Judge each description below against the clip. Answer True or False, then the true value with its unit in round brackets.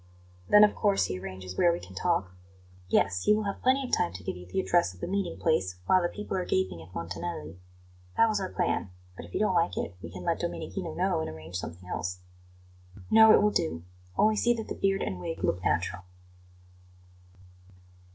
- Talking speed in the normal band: False (210 wpm)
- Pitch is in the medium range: False (95 Hz)